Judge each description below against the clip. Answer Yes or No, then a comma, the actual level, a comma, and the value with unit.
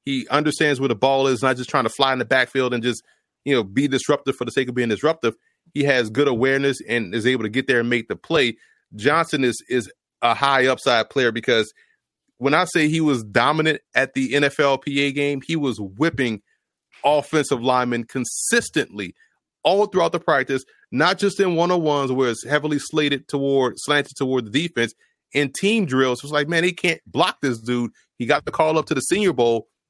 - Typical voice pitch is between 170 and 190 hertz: No, low, 135 Hz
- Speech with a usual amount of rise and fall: Yes, average, 3.3 semitones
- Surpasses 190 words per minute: Yes, fast, 205 wpm